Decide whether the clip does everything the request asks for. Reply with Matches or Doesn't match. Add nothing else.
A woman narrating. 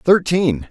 Doesn't match